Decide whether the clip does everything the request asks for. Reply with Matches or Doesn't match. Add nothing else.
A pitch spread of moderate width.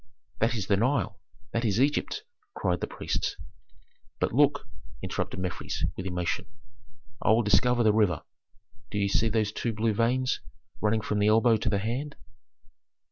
Matches